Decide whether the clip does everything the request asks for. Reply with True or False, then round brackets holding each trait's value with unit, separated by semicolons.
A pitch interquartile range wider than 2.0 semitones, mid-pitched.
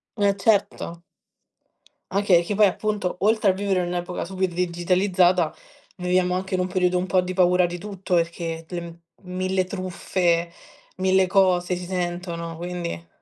False (1.5 semitones; 180 Hz)